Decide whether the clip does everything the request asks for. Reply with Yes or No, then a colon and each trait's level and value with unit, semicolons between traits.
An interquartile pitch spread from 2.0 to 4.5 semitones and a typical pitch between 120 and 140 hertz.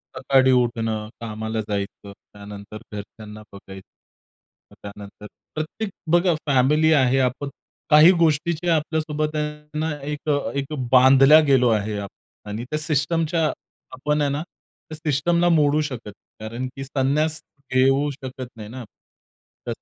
No: wide, 5.4 semitones; low, 135 Hz